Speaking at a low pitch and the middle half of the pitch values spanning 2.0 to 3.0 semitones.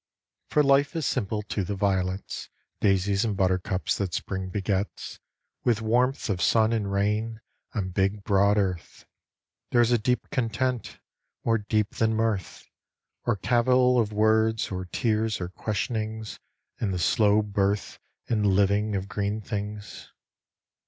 Yes: low, 105 Hz; narrow, 2.4 semitones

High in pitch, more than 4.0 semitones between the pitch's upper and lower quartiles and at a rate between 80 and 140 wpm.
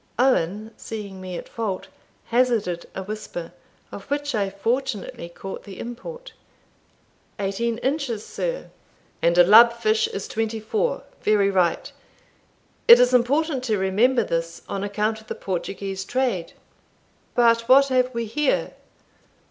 Yes: high, 220 Hz; average, 4.4 semitones; slow, 135 wpm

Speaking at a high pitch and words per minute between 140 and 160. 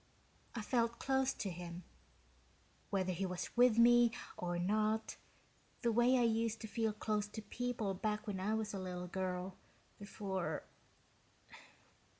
Yes: high, 215 Hz; average, 145 wpm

